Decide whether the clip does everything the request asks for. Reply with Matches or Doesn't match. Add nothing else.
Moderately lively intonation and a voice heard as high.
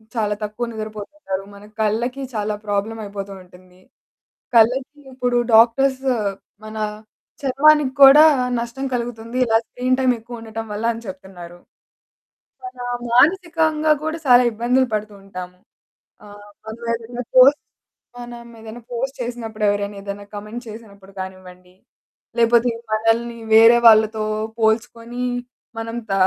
Matches